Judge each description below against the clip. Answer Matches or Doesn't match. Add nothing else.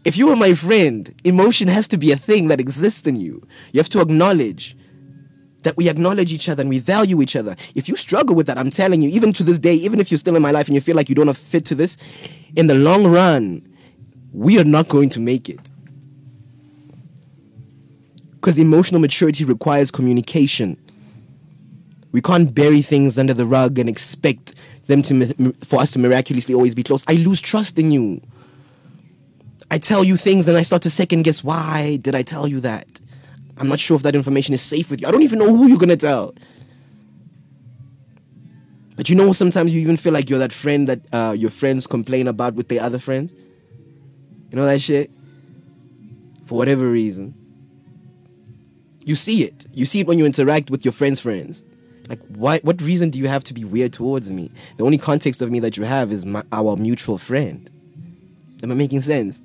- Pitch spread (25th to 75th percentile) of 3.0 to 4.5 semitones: Matches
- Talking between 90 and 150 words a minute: Doesn't match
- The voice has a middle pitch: Matches